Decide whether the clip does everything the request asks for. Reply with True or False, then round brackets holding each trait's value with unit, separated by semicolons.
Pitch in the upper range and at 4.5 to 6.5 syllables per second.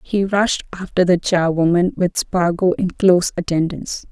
False (180 Hz; 4.8 syllables/s)